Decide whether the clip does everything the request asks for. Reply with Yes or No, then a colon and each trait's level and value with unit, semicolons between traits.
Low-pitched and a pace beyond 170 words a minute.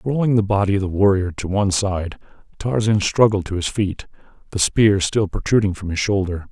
Yes: low, 100 Hz; average, 195 wpm